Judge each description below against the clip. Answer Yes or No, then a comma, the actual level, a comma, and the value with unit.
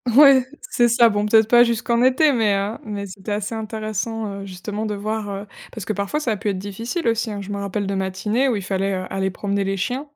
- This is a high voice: Yes, high, 210 Hz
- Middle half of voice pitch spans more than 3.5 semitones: No, narrow, 2.6 semitones